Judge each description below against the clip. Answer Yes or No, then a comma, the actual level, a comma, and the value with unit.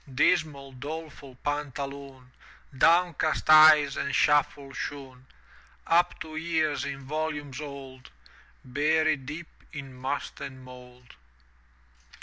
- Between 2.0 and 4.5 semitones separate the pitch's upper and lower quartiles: Yes, average, 2.8 semitones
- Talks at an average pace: No, slow, 105 wpm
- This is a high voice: No, medium, 145 Hz